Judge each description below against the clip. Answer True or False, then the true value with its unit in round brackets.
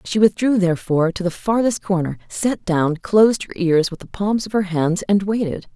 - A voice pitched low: False (190 Hz)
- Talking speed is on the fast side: True (210 wpm)